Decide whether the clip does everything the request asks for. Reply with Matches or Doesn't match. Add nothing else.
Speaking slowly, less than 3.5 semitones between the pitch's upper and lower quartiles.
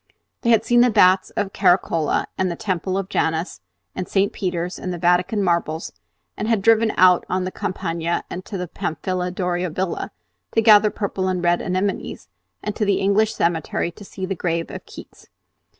Doesn't match